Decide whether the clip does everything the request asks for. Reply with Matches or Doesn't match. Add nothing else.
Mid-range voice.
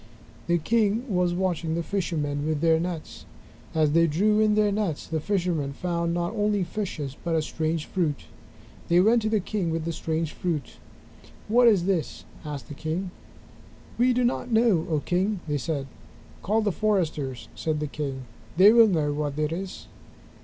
Matches